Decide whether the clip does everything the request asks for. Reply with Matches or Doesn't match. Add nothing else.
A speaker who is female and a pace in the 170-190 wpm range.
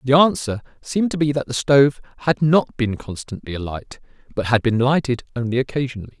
Doesn't match